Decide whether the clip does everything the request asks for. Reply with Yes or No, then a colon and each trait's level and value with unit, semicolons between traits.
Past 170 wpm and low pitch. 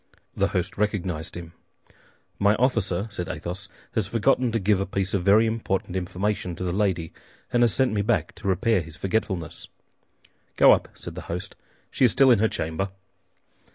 Yes: average, 180 wpm; low, 100 Hz